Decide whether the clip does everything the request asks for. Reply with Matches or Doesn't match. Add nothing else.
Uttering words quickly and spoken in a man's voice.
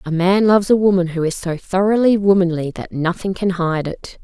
Doesn't match